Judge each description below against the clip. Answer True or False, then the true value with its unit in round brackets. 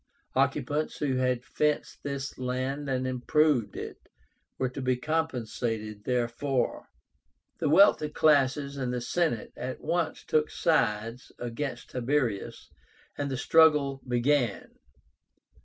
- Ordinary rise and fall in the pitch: True (3.2 semitones)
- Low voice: True (130 Hz)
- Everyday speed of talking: False (115 wpm)